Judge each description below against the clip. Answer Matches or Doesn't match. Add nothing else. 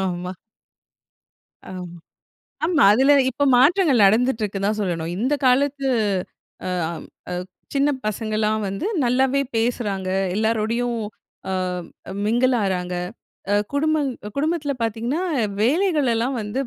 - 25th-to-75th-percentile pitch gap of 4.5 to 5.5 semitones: Matches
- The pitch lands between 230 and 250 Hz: Matches